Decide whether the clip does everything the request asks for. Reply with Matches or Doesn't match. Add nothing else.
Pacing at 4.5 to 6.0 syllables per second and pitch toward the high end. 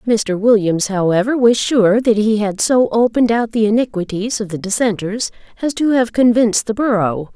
Matches